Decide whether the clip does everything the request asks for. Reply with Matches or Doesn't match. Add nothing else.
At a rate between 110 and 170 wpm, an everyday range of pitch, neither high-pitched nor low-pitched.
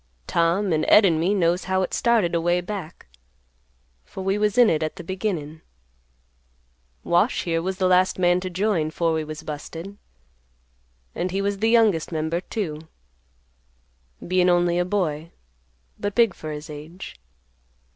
Matches